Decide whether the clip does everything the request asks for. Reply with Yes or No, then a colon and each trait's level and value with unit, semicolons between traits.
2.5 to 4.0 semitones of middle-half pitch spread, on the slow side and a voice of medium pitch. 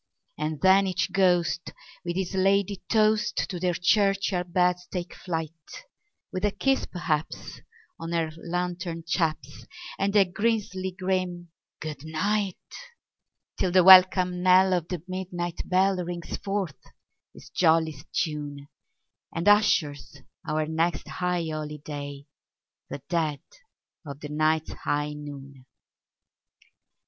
Yes: average, 3.3 semitones; slow, 115 wpm; medium, 175 Hz